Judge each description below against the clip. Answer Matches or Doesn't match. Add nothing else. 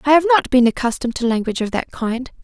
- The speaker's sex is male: Doesn't match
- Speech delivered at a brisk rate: Matches